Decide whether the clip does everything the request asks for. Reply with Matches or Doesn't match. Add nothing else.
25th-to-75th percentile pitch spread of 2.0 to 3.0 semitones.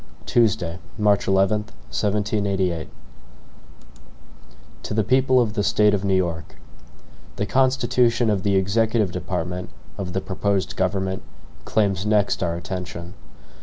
Matches